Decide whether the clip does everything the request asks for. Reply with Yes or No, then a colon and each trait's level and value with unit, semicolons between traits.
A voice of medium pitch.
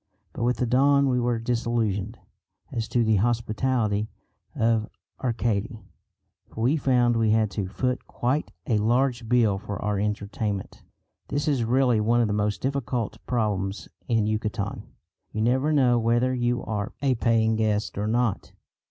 No: low, 115 Hz